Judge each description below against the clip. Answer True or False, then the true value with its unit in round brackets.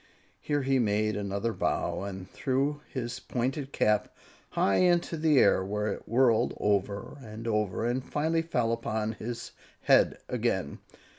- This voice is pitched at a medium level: False (115 Hz)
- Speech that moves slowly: False (150 wpm)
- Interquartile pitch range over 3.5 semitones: True (4.2 semitones)